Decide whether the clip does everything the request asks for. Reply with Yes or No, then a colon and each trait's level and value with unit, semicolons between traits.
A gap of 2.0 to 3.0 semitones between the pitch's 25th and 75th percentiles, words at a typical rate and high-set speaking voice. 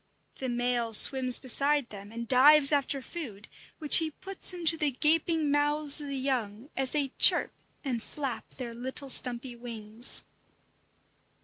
No: average, 3.6 semitones; average, 145 wpm; very high, 265 Hz